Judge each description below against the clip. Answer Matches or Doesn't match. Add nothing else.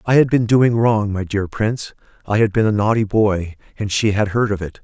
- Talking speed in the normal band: Doesn't match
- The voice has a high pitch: Doesn't match